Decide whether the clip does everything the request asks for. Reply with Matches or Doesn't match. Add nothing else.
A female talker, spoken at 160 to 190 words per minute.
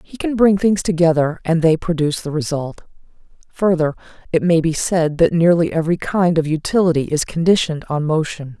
Matches